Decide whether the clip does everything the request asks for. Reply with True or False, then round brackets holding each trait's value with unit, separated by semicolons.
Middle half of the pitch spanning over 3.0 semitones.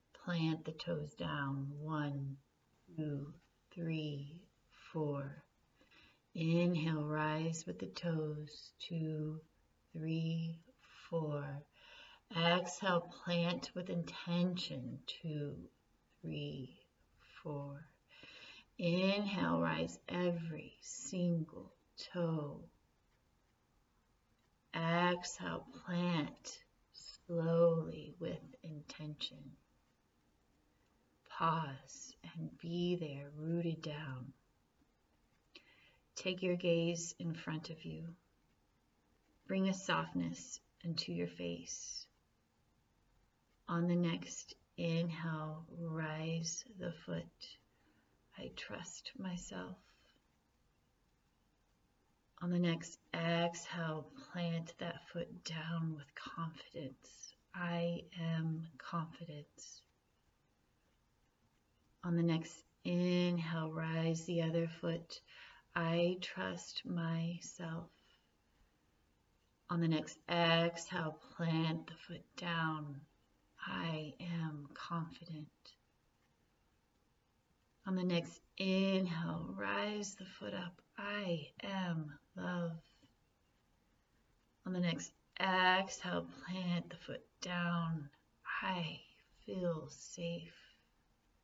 False (2.7 semitones)